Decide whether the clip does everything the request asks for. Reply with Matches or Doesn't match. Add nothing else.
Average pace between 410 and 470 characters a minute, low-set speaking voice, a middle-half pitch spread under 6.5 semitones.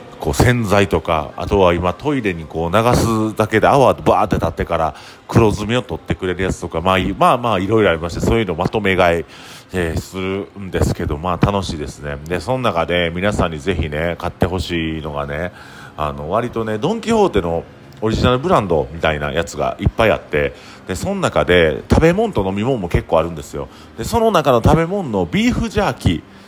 Matches